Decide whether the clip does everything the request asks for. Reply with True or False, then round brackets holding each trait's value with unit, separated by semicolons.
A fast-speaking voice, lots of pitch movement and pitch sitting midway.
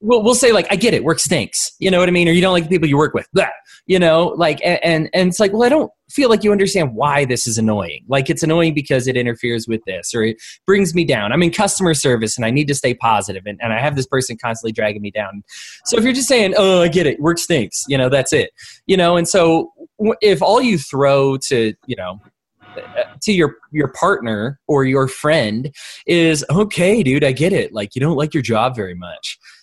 True (245 wpm; 7.4 semitones; 155 Hz)